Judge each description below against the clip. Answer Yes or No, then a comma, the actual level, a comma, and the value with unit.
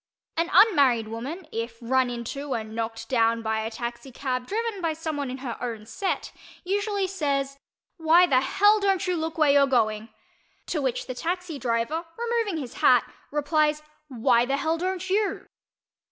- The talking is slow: No, average, 165 wpm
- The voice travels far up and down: Yes, wide, 6.8 semitones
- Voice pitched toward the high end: Yes, very high, 280 Hz